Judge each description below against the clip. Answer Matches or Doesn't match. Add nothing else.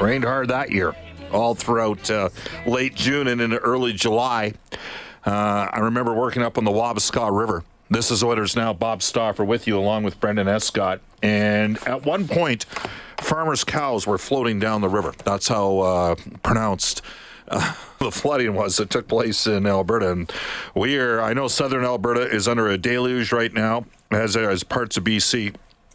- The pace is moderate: Matches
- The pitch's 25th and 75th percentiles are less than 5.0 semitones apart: Matches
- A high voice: Doesn't match